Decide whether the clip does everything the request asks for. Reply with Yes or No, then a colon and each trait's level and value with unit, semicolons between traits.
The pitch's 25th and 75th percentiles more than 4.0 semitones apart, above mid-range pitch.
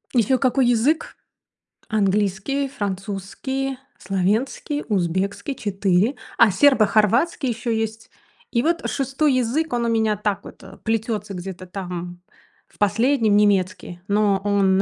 Yes: average, 4.6 semitones; high, 215 Hz